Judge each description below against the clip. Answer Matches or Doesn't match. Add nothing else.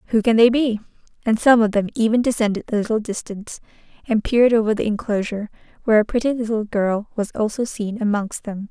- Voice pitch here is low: Doesn't match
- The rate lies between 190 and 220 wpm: Matches